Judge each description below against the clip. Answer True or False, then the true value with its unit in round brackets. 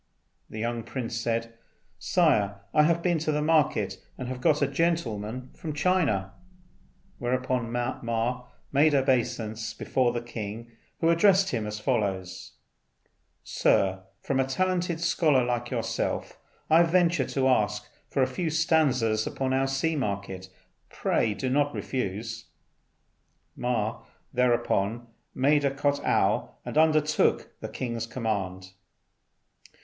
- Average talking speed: False (125 wpm)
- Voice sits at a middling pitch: False (125 Hz)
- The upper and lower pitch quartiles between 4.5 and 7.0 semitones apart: True (5.0 semitones)